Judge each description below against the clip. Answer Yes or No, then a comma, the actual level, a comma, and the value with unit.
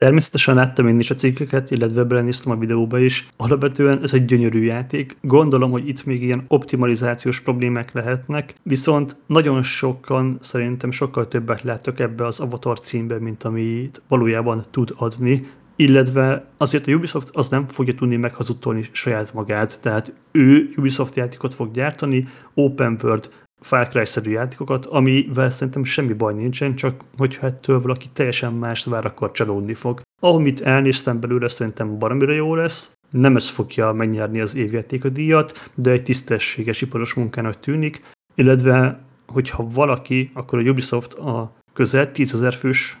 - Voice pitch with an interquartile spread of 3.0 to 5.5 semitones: No, narrow, 2.4 semitones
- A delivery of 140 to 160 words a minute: Yes, average, 150 wpm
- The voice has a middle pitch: No, low, 130 Hz